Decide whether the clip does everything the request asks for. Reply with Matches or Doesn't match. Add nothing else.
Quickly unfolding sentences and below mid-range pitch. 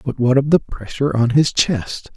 Matches